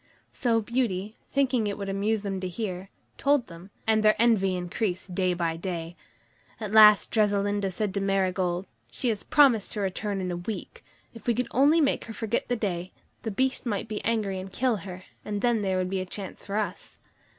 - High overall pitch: Yes, high, 205 Hz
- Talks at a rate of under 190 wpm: No, average, 200 wpm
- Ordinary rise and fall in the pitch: Yes, average, 3.2 semitones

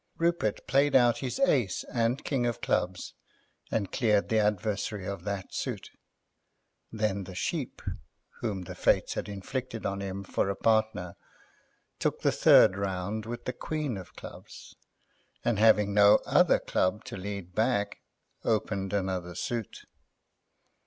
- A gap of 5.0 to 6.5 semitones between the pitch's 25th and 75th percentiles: No, average, 3.2 semitones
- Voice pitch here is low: Yes, low, 105 Hz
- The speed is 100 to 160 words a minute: Yes, average, 140 wpm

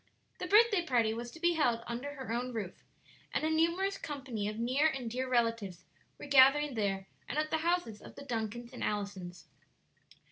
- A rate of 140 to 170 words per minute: No, average, 185 wpm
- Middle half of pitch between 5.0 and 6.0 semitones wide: Yes, wide, 5.4 semitones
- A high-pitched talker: Yes, very high, 250 Hz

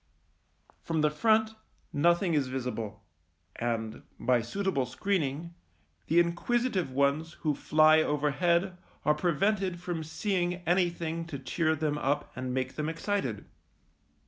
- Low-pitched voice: No, medium, 160 Hz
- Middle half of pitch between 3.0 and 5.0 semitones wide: Yes, average, 4.3 semitones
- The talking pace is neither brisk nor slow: No, slow, 120 wpm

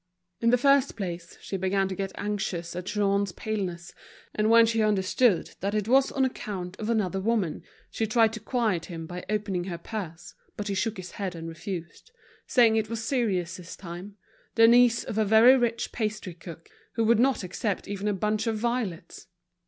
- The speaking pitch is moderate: No, high, 205 Hz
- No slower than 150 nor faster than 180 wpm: No, average, 190 wpm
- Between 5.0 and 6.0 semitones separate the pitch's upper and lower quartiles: No, average, 3.7 semitones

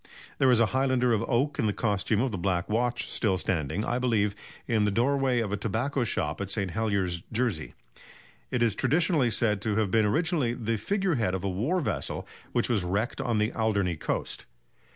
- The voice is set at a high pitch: No, low, 110 Hz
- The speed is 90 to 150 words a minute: No, average, 200 wpm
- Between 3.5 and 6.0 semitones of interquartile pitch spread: Yes, average, 3.8 semitones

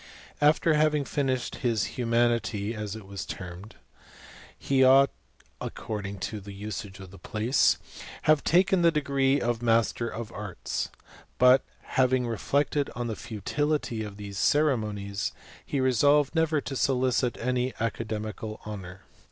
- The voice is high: No, low, 120 Hz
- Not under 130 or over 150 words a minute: Yes, average, 140 wpm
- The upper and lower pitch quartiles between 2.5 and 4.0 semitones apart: No, average, 4.5 semitones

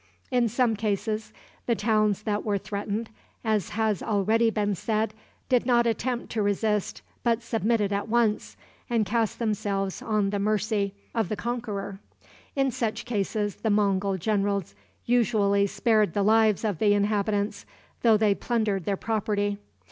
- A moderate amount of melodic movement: No, narrow, 1.9 semitones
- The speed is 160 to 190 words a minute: No, average, 150 wpm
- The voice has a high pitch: Yes, high, 215 Hz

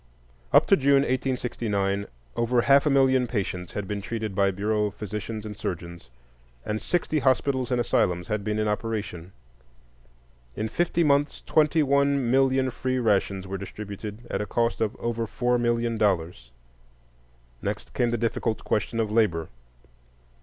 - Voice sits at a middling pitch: No, low, 110 Hz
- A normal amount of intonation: Yes, average, 4.0 semitones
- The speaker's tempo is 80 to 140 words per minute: No, average, 150 wpm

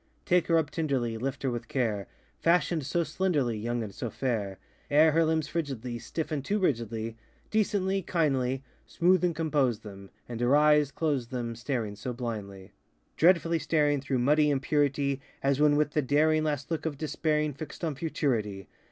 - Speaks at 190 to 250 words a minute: No, average, 165 wpm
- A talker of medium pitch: Yes, medium, 145 Hz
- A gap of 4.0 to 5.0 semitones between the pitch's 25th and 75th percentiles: Yes, average, 4.6 semitones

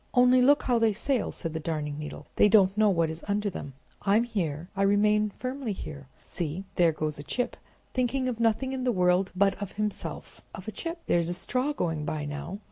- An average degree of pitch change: No, wide, 6.3 semitones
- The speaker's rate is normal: No, fast, 210 wpm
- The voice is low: No, high, 200 Hz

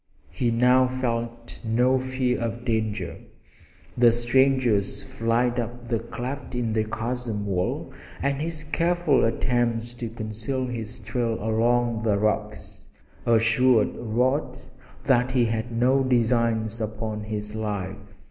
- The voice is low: Yes, low, 120 Hz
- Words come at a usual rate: No, slow, 125 wpm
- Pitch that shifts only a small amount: Yes, narrow, 2.2 semitones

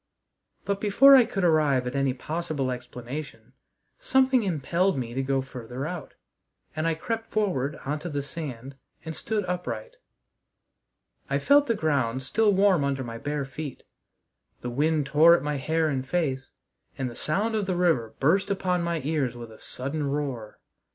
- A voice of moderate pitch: Yes, medium, 150 Hz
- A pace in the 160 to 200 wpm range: Yes, average, 170 wpm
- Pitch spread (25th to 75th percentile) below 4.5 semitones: No, average, 5.3 semitones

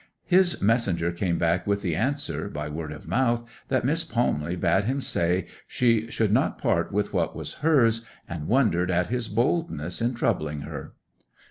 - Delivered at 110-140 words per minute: No, average, 170 wpm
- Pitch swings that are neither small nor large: No, wide, 6.3 semitones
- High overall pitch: No, low, 105 Hz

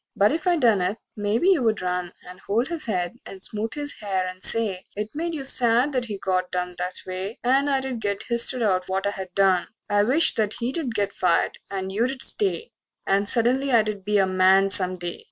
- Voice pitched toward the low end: No, high, 210 Hz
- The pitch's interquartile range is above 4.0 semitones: Yes, average, 5.0 semitones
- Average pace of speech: No, fast, 215 wpm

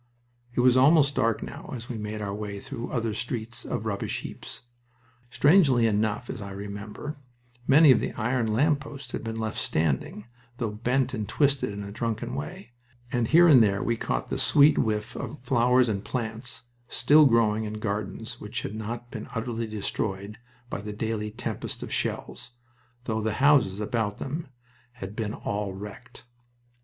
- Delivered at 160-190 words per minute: Yes, average, 170 wpm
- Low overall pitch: Yes, low, 115 Hz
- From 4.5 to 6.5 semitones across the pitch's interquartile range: No, average, 3.1 semitones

